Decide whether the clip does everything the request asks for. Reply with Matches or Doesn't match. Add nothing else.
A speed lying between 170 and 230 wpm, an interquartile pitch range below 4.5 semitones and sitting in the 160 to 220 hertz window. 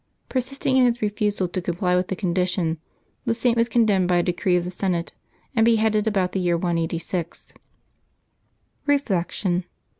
Doesn't match